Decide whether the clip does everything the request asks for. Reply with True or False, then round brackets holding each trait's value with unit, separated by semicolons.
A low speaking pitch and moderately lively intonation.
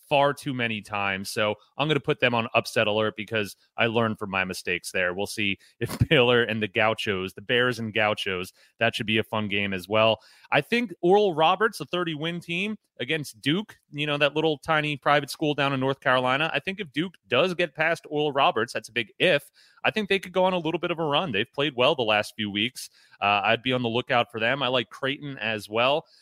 False (130 Hz; 6.4 semitones)